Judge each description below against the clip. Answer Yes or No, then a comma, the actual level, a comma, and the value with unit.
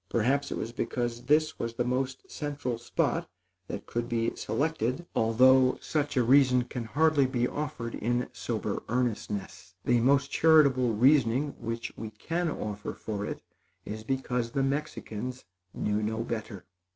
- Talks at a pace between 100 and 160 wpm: Yes, average, 150 wpm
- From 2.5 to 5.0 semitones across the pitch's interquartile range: Yes, average, 3.3 semitones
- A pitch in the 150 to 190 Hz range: No, low, 125 Hz